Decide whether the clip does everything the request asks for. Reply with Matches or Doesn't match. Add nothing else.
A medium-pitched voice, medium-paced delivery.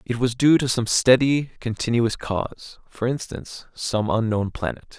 Doesn't match